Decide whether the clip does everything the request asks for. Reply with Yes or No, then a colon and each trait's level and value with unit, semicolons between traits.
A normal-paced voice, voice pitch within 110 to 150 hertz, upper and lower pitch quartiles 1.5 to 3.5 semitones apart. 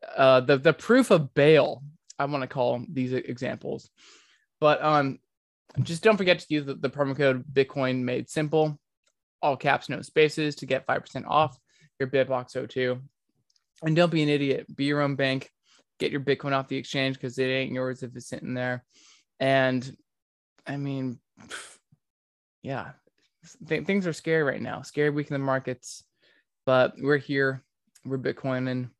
Yes: average, 170 wpm; low, 135 Hz; narrow, 2.4 semitones